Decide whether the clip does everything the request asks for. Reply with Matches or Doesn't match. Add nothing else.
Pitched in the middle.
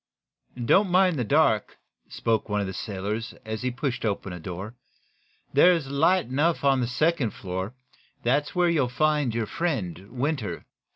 Doesn't match